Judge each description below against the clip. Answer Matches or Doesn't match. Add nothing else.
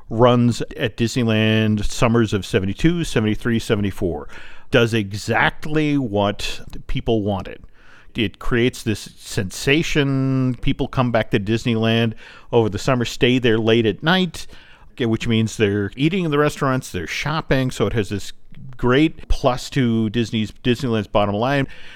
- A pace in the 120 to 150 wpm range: Matches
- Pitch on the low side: Matches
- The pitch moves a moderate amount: Matches